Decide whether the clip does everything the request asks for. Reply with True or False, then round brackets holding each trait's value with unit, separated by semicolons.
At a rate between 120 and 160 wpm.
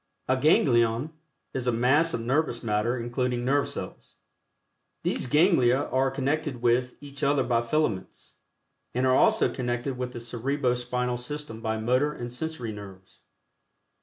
True (145 wpm)